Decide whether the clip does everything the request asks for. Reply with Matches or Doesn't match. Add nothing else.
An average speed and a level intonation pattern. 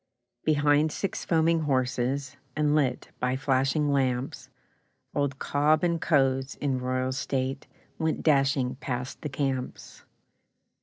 Doesn't match